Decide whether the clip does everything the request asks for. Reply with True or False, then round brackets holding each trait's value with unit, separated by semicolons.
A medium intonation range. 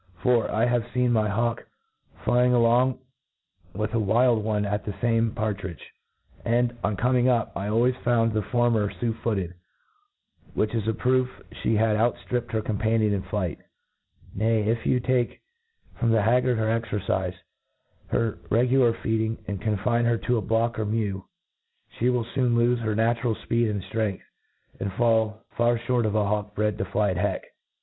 False (2.2 semitones)